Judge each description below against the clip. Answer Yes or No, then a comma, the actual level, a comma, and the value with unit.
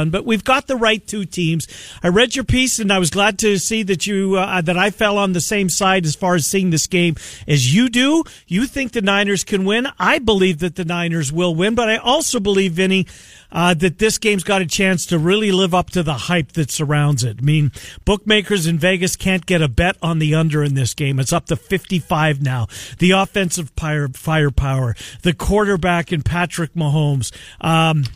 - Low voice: No, medium, 180 Hz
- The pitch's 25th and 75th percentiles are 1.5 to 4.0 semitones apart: No, average, 4.4 semitones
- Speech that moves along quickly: Yes, fast, 215 wpm